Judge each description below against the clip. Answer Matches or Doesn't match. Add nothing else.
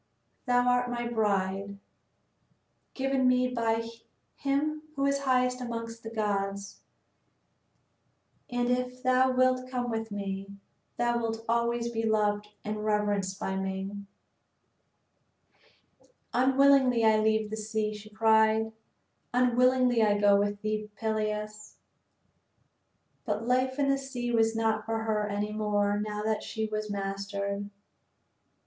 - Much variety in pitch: Doesn't match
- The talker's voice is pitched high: Matches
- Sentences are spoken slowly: Matches